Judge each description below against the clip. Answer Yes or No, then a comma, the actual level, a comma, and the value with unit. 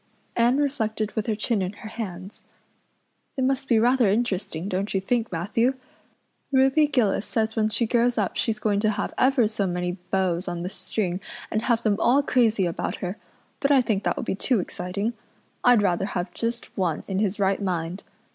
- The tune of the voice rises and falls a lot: No, average, 4.0 semitones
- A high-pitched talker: Yes, high, 215 Hz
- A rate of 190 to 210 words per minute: Yes, average, 195 wpm